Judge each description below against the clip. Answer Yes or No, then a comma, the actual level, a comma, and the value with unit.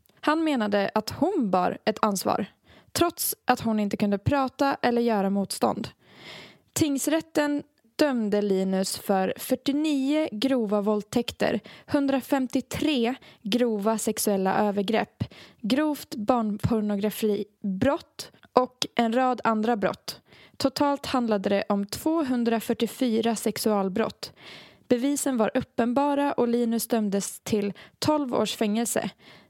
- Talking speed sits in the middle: No, slow, 100 wpm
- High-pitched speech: Yes, high, 235 Hz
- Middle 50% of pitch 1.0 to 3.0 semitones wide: No, average, 4.6 semitones